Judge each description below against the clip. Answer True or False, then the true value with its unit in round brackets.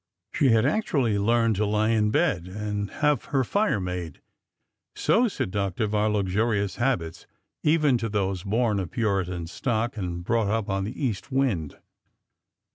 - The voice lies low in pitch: True (105 Hz)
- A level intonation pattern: False (3.6 semitones)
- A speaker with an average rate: True (150 wpm)